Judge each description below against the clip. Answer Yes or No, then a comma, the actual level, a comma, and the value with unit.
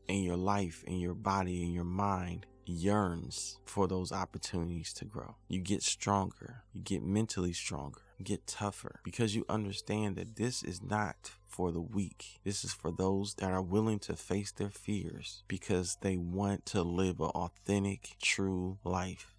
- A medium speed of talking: Yes, average, 170 wpm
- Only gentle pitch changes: Yes, narrow, 2.1 semitones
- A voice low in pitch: Yes, very low, 95 Hz